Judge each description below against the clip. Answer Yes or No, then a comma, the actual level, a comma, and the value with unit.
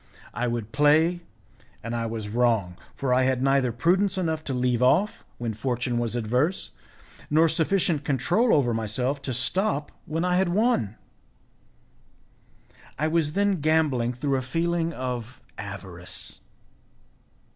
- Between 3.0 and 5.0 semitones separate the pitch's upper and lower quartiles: No, wide, 5.5 semitones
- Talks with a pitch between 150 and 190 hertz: No, low, 135 Hz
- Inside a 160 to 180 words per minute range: No, slow, 135 wpm